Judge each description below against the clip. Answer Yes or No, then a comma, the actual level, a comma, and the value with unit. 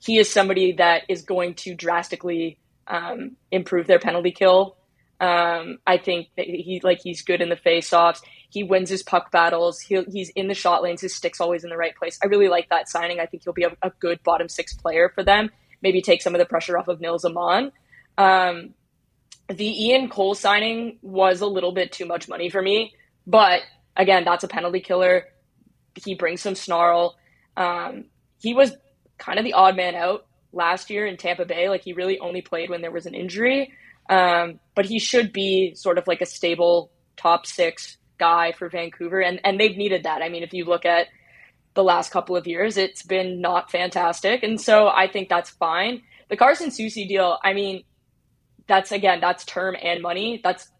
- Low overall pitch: No, medium, 180 Hz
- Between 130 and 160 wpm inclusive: No, average, 200 wpm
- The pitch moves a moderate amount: No, narrow, 2.1 semitones